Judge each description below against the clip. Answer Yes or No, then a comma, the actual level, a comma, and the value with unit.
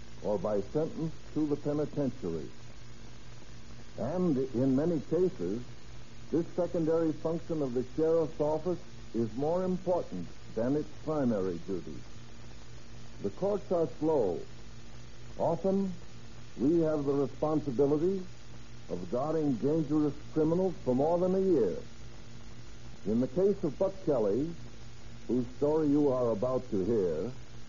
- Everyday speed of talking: No, slow, 120 wpm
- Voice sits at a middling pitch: Yes, medium, 145 Hz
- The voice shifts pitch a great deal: Yes, wide, 5.7 semitones